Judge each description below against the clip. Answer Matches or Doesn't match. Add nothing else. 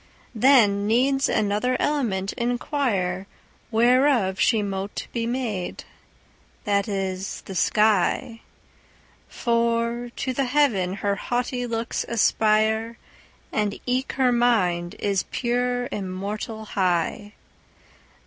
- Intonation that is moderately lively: Matches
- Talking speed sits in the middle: Doesn't match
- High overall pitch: Matches